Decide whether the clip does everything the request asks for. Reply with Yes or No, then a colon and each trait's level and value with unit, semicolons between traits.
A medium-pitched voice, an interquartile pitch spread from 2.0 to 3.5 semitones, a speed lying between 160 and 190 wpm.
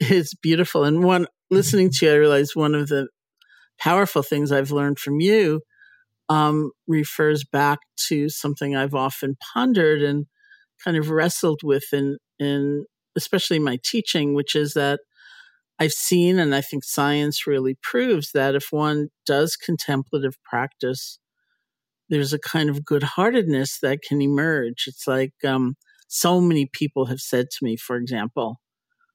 No: medium, 145 Hz; narrow, 2.6 semitones; average, 150 wpm